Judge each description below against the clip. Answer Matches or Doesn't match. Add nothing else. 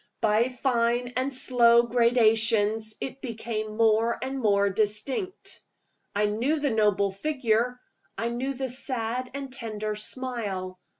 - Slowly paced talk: Matches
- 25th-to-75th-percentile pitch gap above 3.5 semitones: Doesn't match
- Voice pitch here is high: Matches